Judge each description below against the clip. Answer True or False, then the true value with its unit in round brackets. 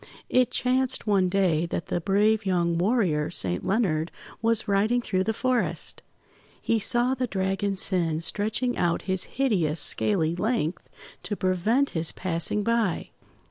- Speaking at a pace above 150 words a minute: False (140 wpm)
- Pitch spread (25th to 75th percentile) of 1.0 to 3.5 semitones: False (4.9 semitones)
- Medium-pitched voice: False (195 Hz)